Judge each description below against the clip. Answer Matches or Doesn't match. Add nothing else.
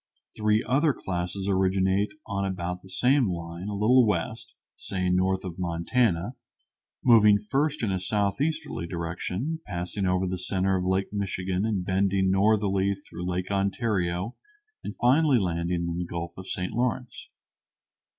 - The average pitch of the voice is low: Matches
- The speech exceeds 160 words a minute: Doesn't match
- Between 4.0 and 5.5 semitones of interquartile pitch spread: Doesn't match